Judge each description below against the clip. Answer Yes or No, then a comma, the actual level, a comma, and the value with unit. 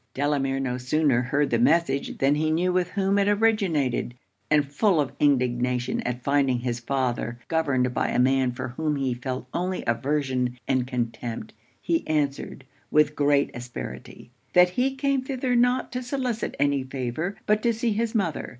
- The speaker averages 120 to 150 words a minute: No, average, 170 wpm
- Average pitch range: No, wide, 6.4 semitones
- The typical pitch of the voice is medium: Yes, medium, 145 Hz